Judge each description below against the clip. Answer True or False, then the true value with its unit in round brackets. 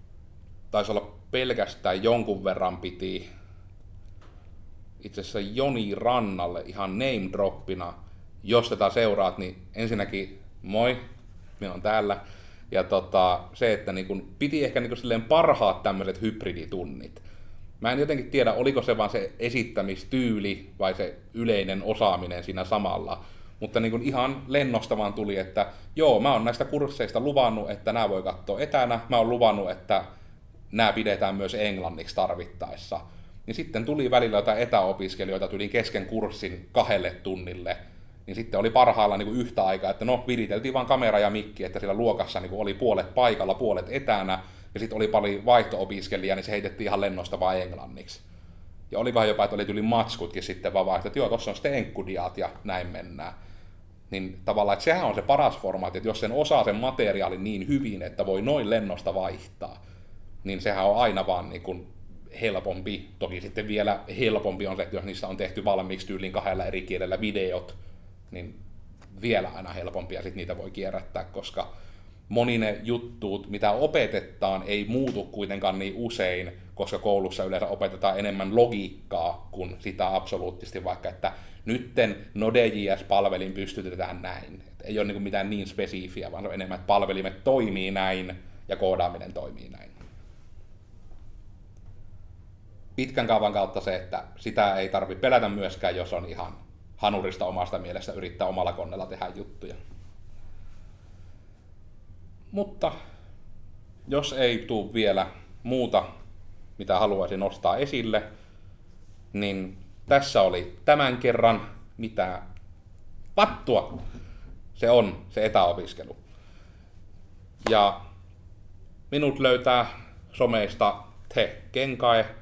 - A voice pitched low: True (95 Hz)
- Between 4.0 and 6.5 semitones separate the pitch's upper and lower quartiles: False (2.8 semitones)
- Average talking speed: True (140 wpm)